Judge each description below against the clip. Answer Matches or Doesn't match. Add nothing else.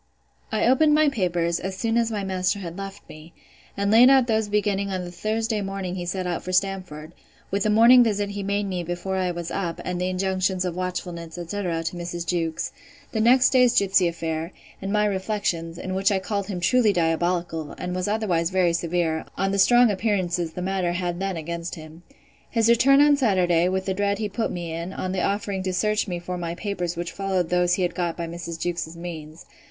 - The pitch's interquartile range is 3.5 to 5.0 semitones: Doesn't match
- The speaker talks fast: Matches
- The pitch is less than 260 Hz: Matches